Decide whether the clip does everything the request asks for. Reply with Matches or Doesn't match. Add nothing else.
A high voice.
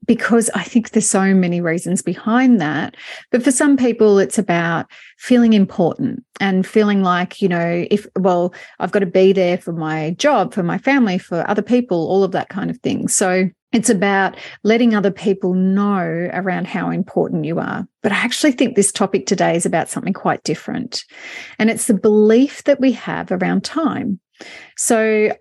Matches